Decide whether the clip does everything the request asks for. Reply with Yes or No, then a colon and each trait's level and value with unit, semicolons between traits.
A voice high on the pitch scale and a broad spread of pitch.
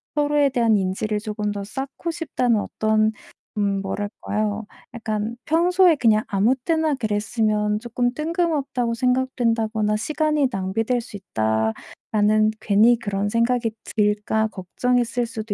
No: high, 225 Hz; average, 3.3 semitones